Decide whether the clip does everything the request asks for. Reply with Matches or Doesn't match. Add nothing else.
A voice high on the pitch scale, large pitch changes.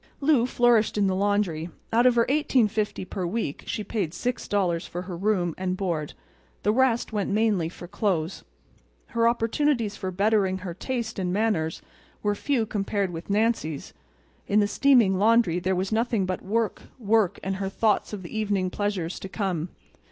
Doesn't match